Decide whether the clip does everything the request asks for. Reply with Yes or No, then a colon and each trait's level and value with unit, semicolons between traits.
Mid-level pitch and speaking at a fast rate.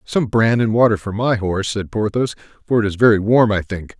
No: low, 110 Hz; fast, 240 wpm